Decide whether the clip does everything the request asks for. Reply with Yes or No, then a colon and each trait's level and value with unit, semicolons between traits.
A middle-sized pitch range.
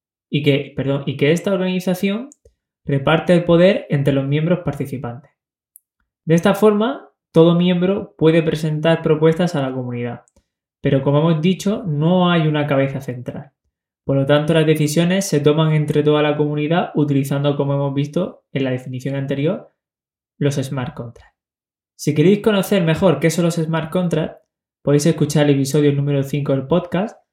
Yes: average, 3.4 semitones